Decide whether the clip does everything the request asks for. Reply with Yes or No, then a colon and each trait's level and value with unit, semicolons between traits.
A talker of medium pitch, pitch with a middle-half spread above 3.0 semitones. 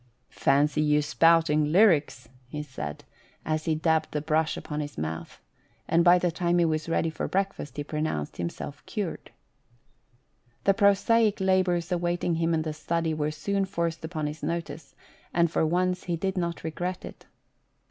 No: medium, 165 Hz; average, 2.7 semitones